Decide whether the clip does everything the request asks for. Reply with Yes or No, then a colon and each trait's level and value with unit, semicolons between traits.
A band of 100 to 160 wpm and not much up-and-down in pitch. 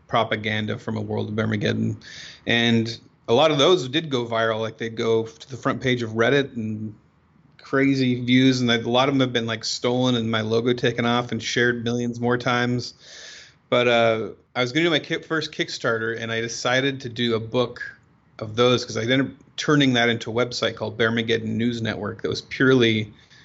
No: fast, 205 wpm; narrow, 2.0 semitones